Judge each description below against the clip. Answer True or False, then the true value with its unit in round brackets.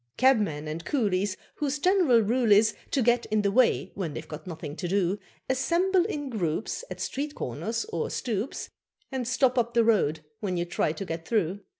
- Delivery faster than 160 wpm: True (190 wpm)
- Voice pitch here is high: True (215 Hz)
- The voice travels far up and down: True (6.7 semitones)